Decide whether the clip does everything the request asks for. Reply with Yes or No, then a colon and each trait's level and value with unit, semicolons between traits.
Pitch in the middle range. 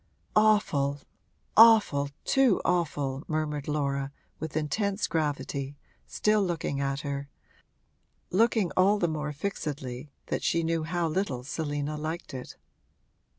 Yes: medium, 155 Hz